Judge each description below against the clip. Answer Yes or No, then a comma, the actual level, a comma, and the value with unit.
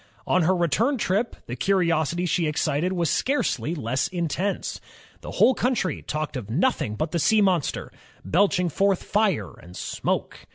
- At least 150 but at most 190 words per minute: Yes, average, 165 wpm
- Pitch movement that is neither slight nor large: Yes, average, 4.5 semitones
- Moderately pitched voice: Yes, medium, 175 Hz